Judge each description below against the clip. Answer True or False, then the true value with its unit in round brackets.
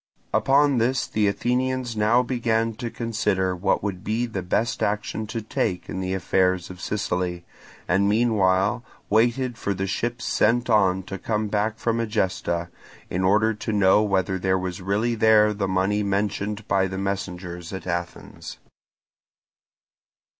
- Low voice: True (105 Hz)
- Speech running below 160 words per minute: True (150 wpm)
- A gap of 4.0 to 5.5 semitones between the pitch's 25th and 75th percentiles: False (3.3 semitones)